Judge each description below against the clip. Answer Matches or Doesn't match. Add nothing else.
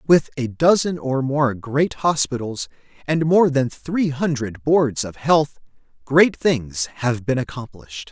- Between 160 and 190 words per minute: Doesn't match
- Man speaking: Matches